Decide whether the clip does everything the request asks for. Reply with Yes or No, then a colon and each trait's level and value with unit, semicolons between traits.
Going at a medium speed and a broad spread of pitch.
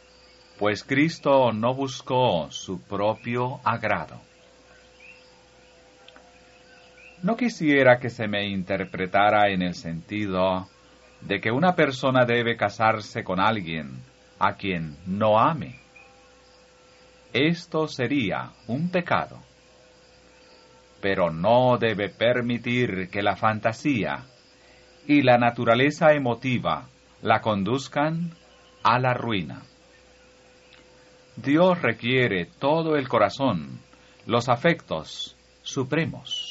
No: slow, 90 wpm; wide, 5.8 semitones